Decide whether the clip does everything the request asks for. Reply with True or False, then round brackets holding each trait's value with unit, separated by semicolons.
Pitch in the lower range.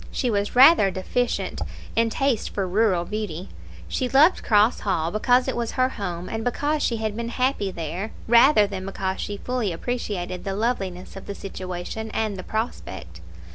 False (210 Hz)